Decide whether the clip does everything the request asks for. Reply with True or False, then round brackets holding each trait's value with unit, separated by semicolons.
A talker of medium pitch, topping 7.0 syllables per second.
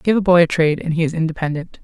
True (165 Hz; 7.3 syllables/s)